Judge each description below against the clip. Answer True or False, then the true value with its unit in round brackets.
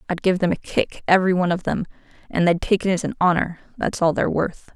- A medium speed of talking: False (240 wpm)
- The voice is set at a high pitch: False (180 Hz)